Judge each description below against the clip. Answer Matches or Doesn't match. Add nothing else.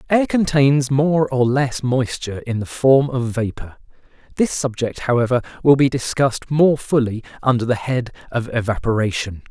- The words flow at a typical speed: Matches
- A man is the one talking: Matches